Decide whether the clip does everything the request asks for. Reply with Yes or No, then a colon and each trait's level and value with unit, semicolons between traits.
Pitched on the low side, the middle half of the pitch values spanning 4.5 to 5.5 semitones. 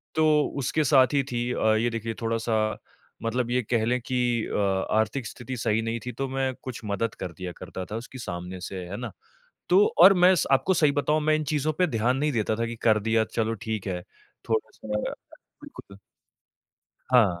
No: low, 115 Hz; average, 3.9 semitones